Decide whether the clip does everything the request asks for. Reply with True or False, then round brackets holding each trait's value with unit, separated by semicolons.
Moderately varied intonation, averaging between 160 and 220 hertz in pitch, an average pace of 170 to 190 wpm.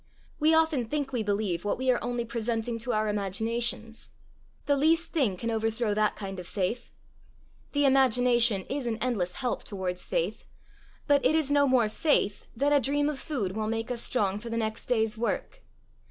False (4.1 semitones; 235 Hz; 185 wpm)